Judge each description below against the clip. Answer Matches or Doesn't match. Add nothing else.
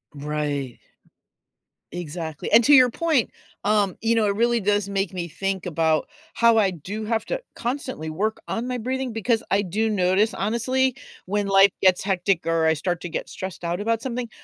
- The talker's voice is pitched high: Matches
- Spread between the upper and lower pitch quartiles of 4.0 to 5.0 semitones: Matches